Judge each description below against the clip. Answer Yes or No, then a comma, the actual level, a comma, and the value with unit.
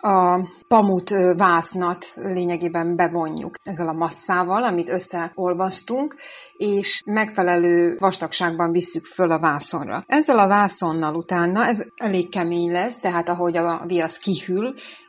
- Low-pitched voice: No, medium, 180 Hz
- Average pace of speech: Yes, average, 120 wpm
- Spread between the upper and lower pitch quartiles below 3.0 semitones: Yes, narrow, 2.5 semitones